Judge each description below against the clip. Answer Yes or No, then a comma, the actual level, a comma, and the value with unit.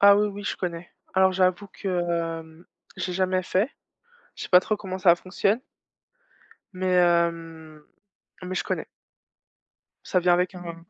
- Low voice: No, medium, 185 Hz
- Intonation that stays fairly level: Yes, narrow, 1.8 semitones